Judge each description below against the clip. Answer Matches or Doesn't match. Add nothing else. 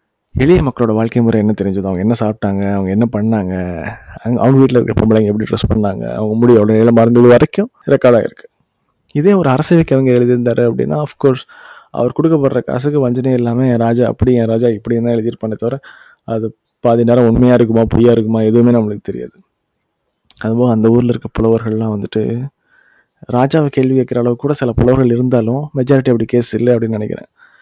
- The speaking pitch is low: Matches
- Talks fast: Matches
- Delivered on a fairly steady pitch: Matches